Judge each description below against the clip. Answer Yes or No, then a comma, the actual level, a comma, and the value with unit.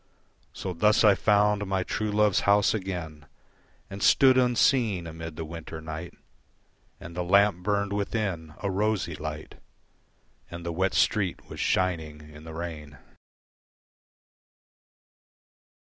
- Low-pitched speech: Yes, very low, 90 Hz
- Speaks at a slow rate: Yes, slow, 125 wpm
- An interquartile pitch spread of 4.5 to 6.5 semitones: No, average, 4.1 semitones